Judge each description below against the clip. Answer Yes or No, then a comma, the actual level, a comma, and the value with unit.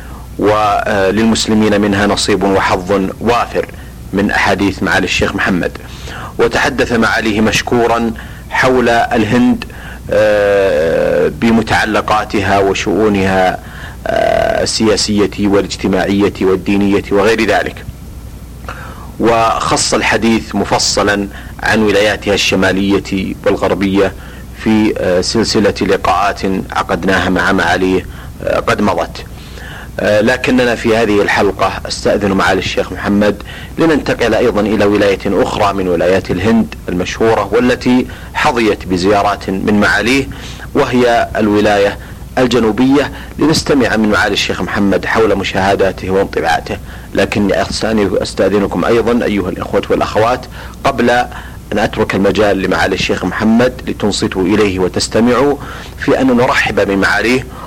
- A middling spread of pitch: Yes, average, 3.1 semitones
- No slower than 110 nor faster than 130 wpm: No, average, 100 wpm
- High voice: No, low, 105 Hz